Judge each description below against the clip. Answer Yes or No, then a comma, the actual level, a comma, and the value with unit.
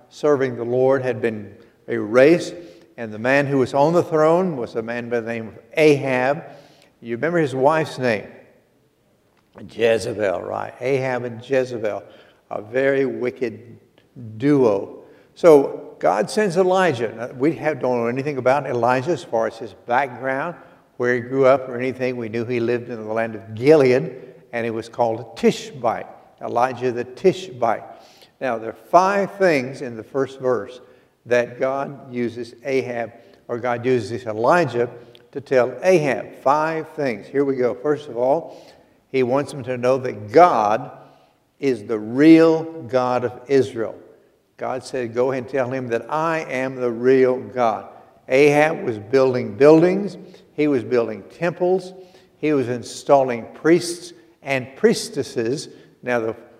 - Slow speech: No, average, 155 wpm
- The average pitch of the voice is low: Yes, low, 130 Hz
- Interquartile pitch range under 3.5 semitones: No, average, 4.0 semitones